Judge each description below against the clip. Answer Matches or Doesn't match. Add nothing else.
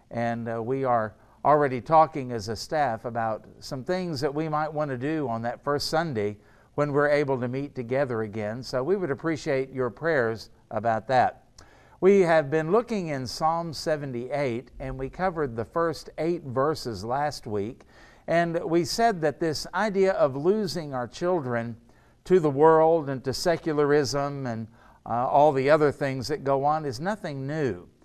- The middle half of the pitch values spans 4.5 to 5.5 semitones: Matches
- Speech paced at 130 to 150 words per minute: Doesn't match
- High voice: Doesn't match